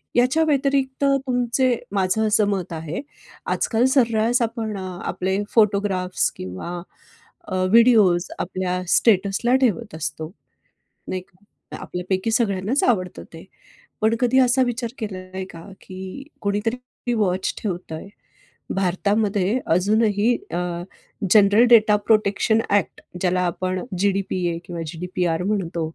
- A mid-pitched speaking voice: No, high, 205 Hz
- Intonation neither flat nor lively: Yes, average, 4.0 semitones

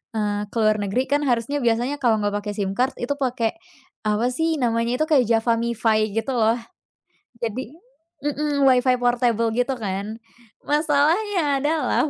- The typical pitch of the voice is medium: No, high, 245 Hz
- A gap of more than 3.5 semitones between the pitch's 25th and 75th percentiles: Yes, average, 4.2 semitones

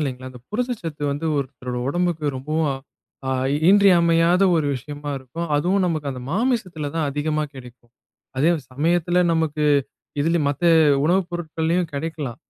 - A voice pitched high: No, medium, 160 Hz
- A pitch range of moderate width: Yes, average, 3.5 semitones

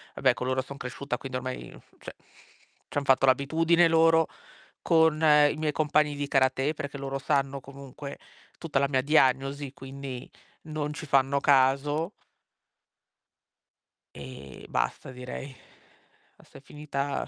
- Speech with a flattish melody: Yes, narrow, 2.0 semitones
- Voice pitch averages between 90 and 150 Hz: Yes, medium, 140 Hz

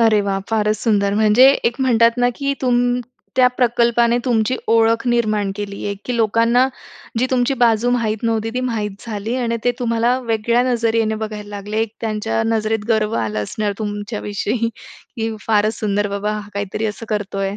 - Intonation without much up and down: Yes, narrow, 2.1 semitones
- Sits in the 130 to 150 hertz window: No, high, 225 Hz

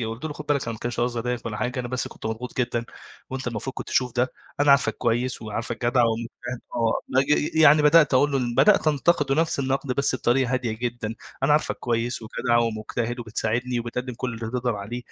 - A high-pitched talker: No, low, 125 Hz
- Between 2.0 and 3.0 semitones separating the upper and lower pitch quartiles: Yes, narrow, 2.5 semitones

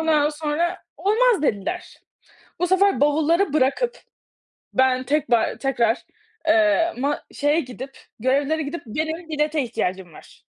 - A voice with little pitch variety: No, average, 4.1 semitones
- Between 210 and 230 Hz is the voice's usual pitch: No, very high, 295 Hz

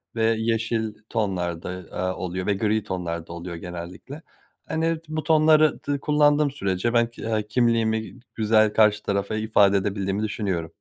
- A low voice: Yes, low, 110 Hz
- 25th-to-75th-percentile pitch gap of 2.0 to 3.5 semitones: No, average, 3.9 semitones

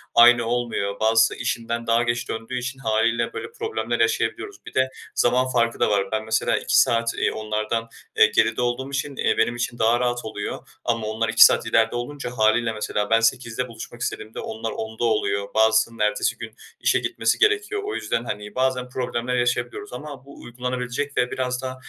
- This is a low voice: Yes, low, 120 Hz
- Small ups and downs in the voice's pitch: Yes, narrow, 2.2 semitones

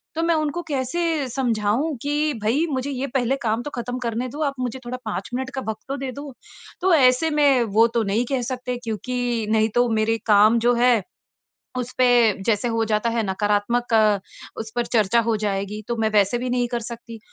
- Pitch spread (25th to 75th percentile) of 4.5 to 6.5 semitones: No, average, 2.9 semitones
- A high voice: Yes, high, 240 Hz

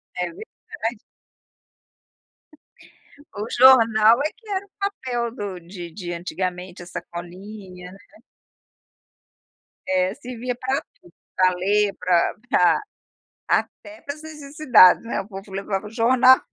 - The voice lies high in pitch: Yes, high, 210 Hz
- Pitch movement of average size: No, wide, 6.0 semitones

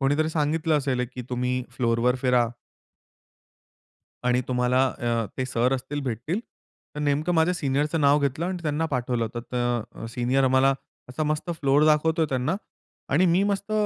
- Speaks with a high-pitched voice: No, low, 135 Hz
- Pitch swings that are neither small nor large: Yes, average, 3.7 semitones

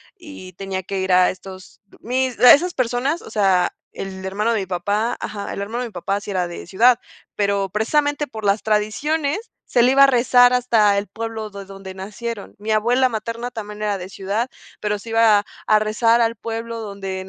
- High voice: Yes, high, 215 Hz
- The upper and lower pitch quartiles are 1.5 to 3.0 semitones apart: No, average, 3.4 semitones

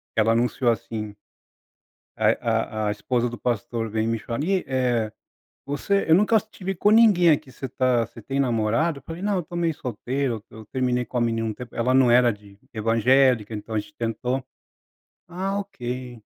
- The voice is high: No, low, 125 Hz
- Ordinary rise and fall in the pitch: Yes, average, 4.8 semitones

